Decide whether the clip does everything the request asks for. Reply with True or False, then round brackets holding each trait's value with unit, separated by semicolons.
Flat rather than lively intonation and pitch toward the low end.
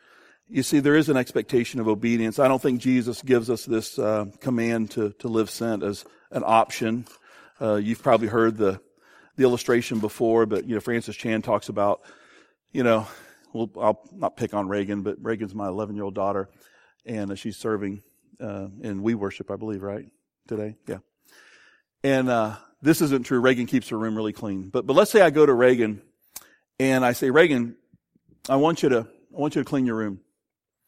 False (3.0 semitones; 115 Hz)